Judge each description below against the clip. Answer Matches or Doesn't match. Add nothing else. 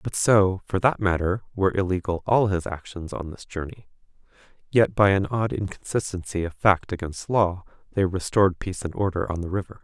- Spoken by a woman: Doesn't match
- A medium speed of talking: Matches